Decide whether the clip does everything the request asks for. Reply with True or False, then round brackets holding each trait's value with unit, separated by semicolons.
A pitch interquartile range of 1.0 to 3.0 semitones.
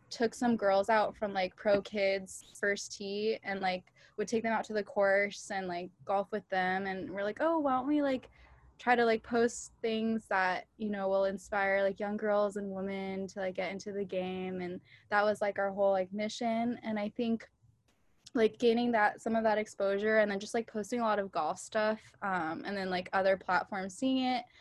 True (2.5 semitones)